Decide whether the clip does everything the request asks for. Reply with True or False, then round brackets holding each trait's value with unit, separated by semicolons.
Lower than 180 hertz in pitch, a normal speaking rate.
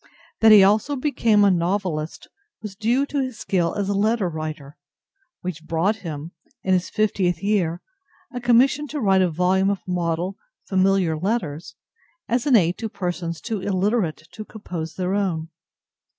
False (190 Hz; 160 wpm)